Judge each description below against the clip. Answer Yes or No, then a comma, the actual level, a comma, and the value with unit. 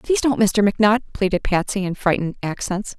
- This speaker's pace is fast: No, average, 180 wpm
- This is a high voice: Yes, high, 200 Hz